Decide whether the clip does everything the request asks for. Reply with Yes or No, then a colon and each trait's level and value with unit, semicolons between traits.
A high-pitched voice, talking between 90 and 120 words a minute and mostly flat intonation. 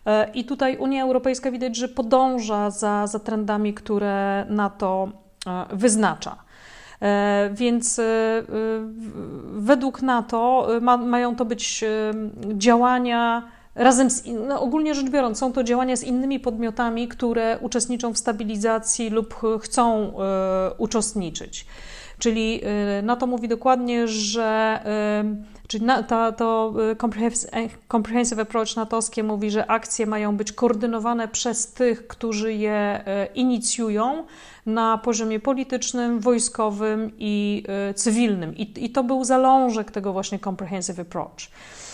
Yes: high, 225 Hz; average, 115 wpm; narrow, 2.3 semitones